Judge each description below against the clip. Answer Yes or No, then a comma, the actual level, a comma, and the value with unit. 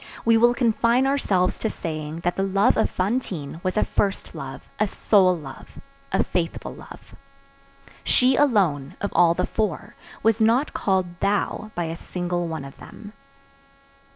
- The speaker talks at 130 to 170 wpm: Yes, average, 155 wpm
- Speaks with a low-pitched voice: No, high, 190 Hz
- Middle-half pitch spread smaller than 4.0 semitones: No, average, 4.8 semitones